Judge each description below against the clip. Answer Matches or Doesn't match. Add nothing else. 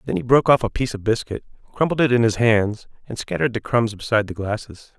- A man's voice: Matches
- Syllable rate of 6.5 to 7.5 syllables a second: Matches